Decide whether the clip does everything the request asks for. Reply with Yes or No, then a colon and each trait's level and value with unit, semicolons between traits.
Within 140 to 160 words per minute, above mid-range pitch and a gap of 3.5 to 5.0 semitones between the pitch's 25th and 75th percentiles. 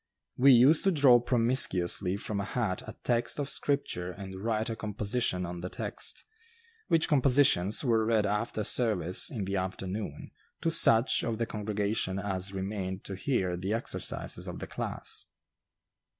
No: average, 155 wpm; low, 105 Hz; average, 4.3 semitones